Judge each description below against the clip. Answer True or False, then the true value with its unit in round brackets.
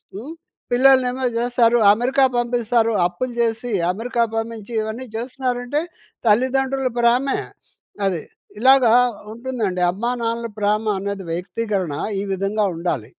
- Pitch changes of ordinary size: True (3.2 semitones)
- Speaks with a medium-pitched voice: False (230 Hz)